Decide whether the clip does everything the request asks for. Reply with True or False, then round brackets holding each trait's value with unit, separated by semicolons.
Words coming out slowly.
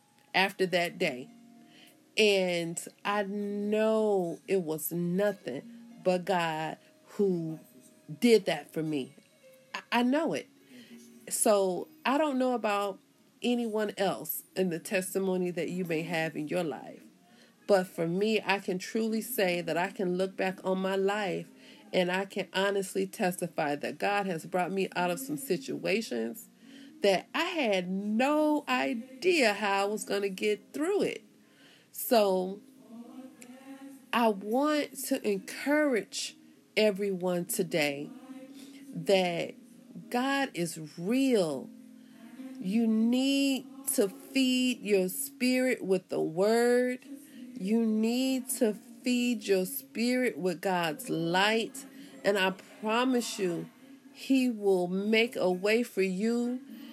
True (125 wpm)